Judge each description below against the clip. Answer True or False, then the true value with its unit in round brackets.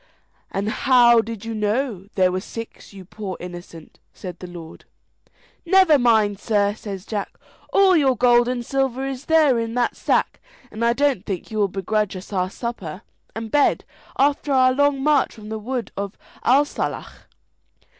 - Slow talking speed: False (165 wpm)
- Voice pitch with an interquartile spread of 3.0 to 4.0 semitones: False (4.8 semitones)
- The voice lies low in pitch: False (230 Hz)